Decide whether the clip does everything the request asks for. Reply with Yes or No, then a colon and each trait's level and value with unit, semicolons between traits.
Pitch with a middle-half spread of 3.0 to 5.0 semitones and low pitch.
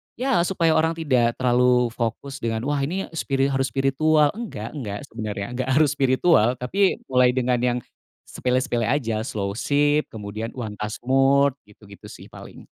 Yes: average, 3.8 semitones; low, 130 Hz